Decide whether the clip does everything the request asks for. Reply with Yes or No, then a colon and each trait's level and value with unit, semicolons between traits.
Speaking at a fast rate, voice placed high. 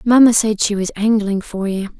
Yes: fast, 210 wpm; high, 210 Hz